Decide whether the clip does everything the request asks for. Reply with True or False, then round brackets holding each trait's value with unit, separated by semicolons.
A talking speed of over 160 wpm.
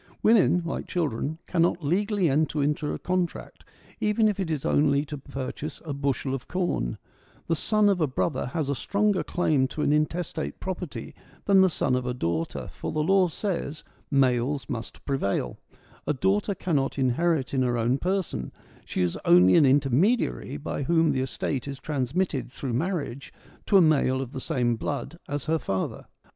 True (180 wpm)